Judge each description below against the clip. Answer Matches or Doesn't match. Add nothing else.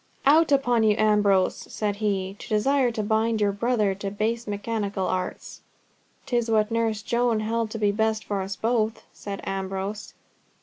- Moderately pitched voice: Doesn't match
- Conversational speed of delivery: Matches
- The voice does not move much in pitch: Matches